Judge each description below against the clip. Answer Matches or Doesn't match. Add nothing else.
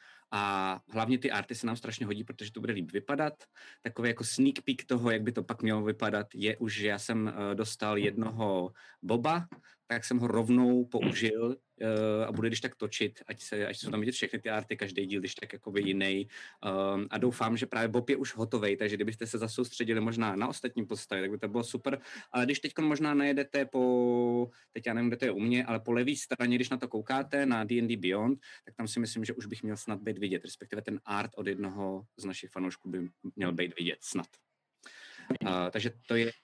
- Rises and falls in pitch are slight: Doesn't match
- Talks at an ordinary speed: Doesn't match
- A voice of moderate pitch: Doesn't match